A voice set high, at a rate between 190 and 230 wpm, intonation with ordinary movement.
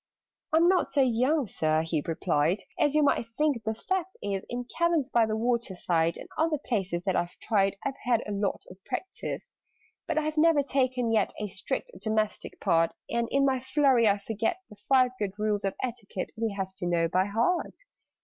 No: high, 225 Hz; average, 195 wpm; wide, 6.0 semitones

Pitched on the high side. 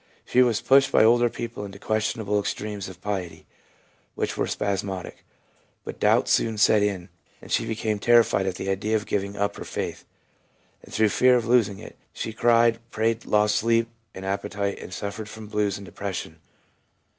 No: low, 105 Hz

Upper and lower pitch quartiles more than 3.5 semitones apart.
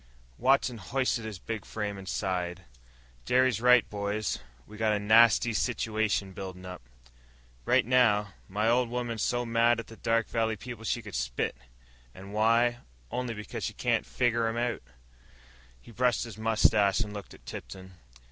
No: average, 2.7 semitones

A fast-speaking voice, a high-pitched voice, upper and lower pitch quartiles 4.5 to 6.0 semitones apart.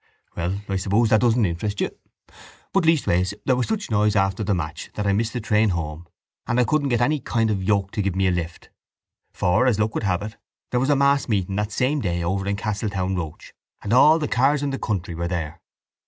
No: fast, 230 wpm; low, 105 Hz; average, 4.8 semitones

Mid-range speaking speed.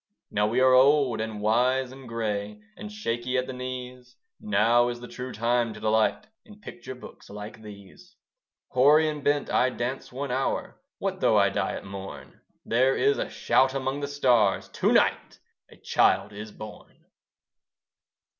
Yes: average, 165 wpm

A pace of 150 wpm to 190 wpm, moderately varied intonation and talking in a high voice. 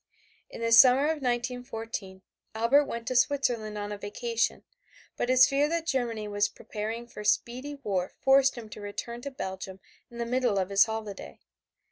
Yes: average, 170 wpm; average, 3.5 semitones; high, 235 Hz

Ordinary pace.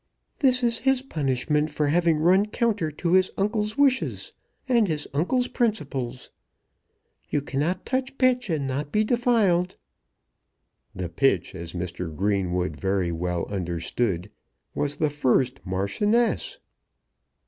No: slow, 125 wpm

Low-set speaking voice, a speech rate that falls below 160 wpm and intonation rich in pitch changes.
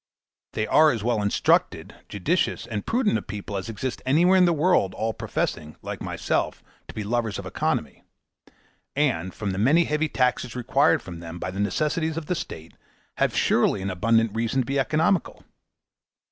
No: low, 120 Hz; average, 175 wpm; wide, 7.0 semitones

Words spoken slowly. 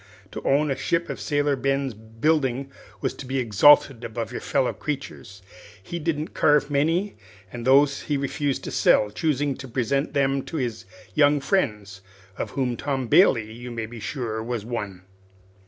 No: average, 170 wpm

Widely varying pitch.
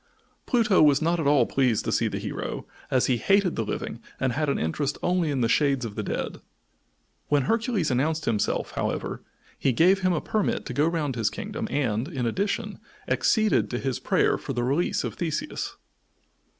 Yes: wide, 5.9 semitones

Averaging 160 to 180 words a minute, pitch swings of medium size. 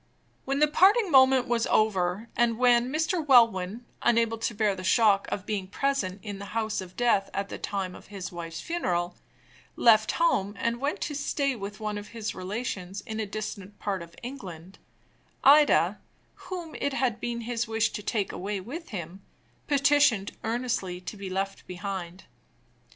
Yes: average, 170 wpm; average, 4.4 semitones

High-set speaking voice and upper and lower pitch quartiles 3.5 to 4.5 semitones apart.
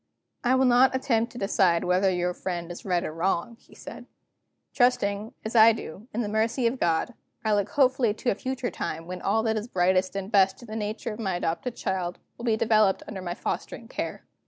Yes: high, 210 Hz; average, 4.2 semitones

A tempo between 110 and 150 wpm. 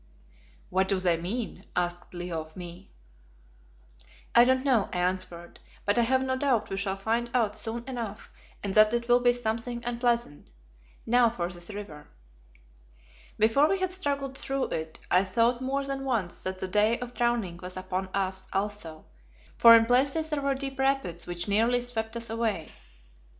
No: average, 170 wpm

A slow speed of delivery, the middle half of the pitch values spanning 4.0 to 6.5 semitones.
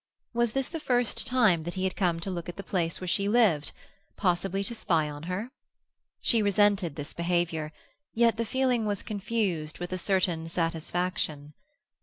No: average, 170 wpm; average, 4.4 semitones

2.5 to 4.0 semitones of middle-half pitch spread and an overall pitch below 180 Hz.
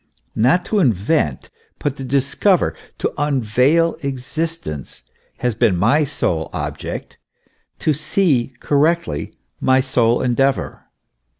No: average, 4.6 semitones; low, 135 Hz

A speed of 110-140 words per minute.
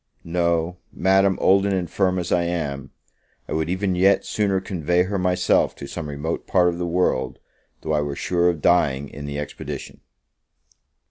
No: average, 175 wpm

